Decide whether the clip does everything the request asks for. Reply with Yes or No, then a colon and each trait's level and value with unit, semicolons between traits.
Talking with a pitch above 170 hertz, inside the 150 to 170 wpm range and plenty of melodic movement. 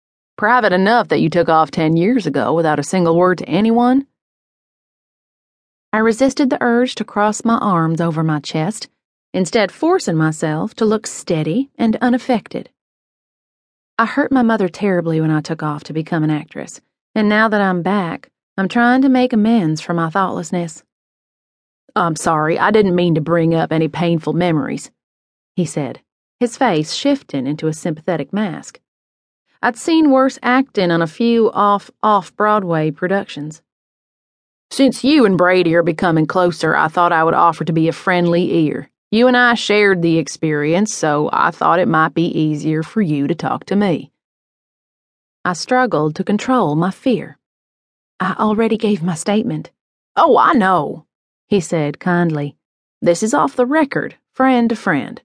Yes: medium, 185 Hz; average, 165 wpm; wide, 5.9 semitones